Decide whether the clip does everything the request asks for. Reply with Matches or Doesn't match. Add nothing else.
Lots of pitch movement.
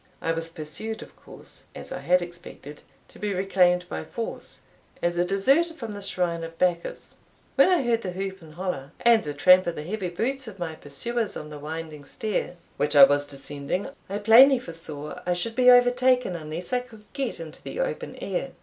Matches